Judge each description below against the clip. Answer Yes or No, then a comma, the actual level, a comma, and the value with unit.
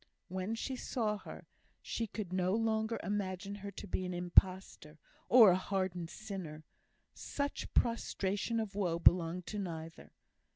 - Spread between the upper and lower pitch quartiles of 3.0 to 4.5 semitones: Yes, average, 3.3 semitones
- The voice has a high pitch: Yes, high, 195 Hz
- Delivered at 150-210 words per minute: No, average, 140 wpm